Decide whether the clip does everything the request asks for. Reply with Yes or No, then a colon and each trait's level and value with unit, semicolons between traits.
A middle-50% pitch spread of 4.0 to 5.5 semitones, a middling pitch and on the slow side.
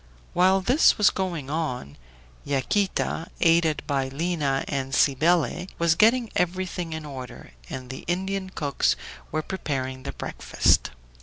Yes: average, 5.2 semitones; medium, 165 Hz; slow, 130 wpm